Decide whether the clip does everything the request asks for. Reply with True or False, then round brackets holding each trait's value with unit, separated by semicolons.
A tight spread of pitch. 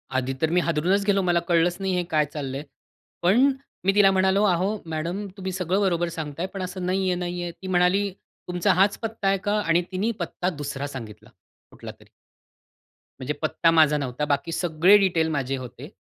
False (3.6 semitones)